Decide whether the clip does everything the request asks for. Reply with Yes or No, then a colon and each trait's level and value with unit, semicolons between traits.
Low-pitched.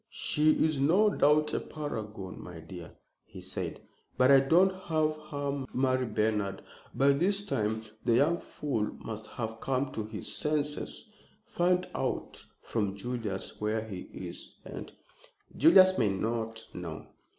Yes: low, 130 Hz